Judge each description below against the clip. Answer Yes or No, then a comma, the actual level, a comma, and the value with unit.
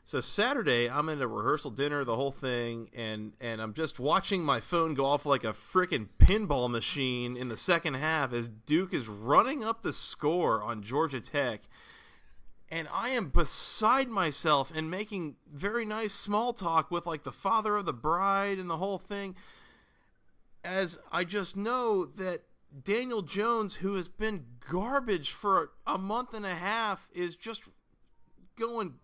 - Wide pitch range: Yes, wide, 6.7 semitones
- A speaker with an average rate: Yes, average, 165 wpm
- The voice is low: No, medium, 175 Hz